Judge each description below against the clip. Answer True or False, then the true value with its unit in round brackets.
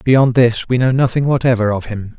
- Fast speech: True (220 wpm)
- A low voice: True (120 Hz)